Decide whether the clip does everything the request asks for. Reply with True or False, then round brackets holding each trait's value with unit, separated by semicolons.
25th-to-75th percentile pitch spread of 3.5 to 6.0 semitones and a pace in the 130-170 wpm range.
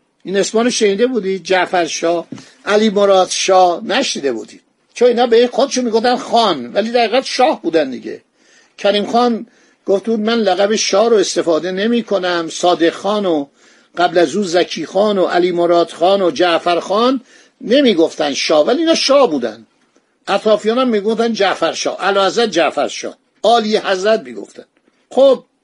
True (4.6 semitones; 155 wpm)